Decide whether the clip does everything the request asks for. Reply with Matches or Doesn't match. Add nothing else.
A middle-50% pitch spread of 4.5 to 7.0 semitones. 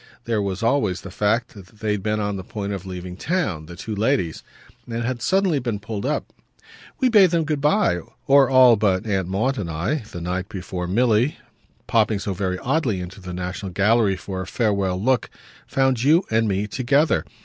Matches